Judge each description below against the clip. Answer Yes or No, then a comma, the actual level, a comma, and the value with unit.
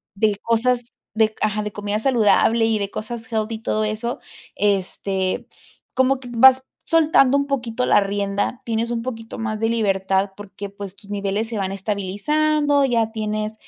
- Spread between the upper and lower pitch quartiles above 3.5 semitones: No, average, 2.8 semitones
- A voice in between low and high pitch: No, high, 220 Hz